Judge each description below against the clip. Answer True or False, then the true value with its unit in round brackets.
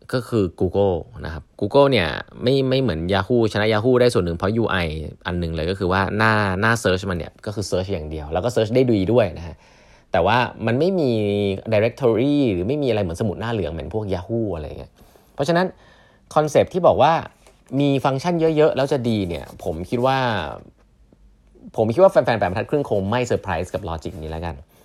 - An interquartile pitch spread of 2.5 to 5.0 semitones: False (5.5 semitones)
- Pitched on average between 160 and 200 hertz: False (105 Hz)